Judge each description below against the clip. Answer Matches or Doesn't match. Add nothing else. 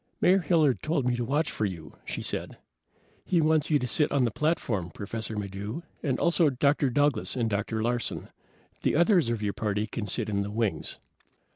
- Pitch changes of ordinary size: Doesn't match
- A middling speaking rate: Matches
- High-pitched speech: Doesn't match